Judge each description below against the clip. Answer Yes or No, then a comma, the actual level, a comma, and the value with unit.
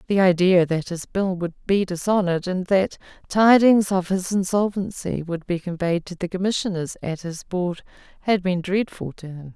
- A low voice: No, medium, 185 Hz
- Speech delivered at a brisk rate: No, average, 175 wpm